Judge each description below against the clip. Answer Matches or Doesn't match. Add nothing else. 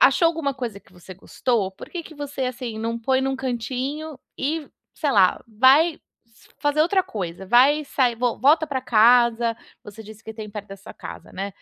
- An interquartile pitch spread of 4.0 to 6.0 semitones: Matches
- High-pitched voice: Matches